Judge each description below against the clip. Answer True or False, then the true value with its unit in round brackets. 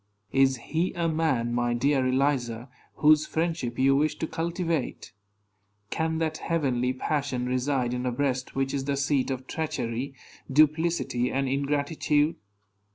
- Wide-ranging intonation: False (3.4 semitones)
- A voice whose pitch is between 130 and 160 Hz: True (140 Hz)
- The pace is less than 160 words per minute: True (140 wpm)